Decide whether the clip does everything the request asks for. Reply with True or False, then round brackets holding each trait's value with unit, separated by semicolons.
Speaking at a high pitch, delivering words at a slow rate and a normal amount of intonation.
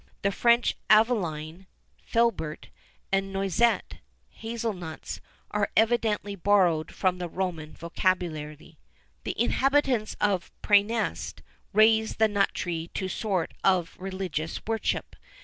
True (195 Hz; 115 wpm; 4.0 semitones)